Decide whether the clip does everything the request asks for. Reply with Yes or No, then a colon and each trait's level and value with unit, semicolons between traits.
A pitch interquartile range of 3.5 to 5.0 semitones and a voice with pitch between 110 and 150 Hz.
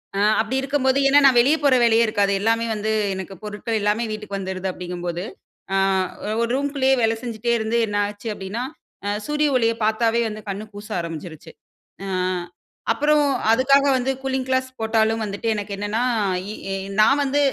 No: average, 4.1 semitones; high, 225 Hz